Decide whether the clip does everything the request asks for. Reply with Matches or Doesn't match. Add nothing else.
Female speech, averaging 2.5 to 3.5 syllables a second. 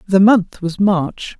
Matches